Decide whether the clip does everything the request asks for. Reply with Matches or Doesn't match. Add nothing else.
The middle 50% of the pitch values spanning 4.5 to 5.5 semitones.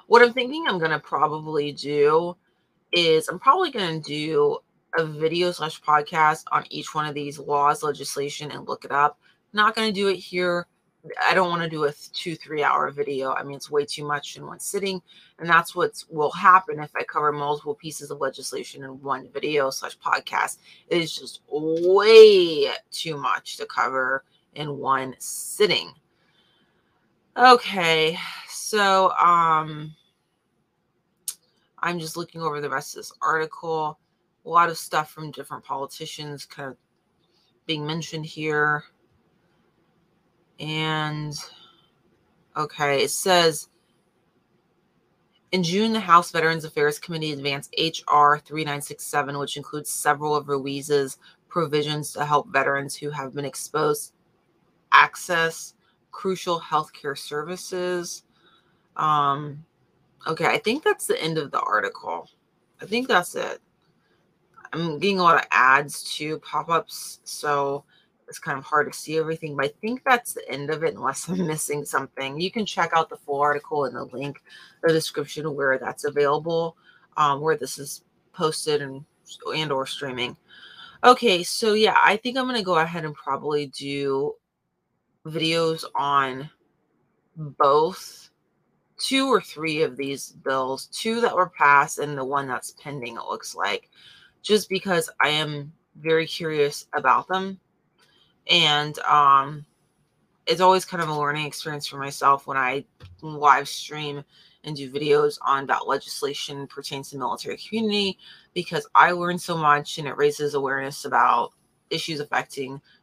Doesn't match